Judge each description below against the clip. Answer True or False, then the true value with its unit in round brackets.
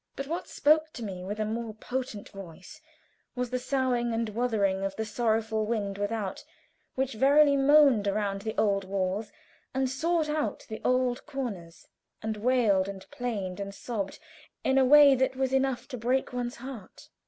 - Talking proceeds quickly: False (170 wpm)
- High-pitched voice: True (235 Hz)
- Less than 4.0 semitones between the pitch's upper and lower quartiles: False (4.6 semitones)